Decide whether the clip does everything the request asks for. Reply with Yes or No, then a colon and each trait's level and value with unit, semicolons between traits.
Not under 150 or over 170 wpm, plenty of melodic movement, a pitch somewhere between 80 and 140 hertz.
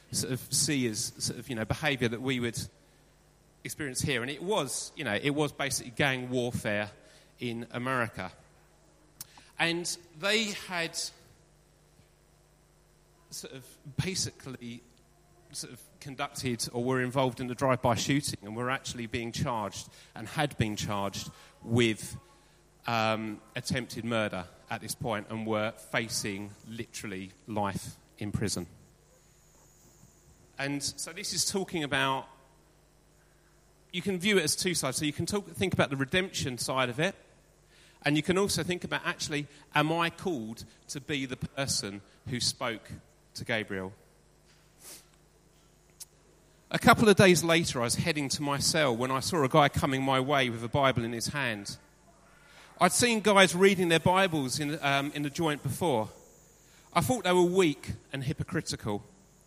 Yes: average, 155 wpm; wide, 5.8 semitones; low, 135 Hz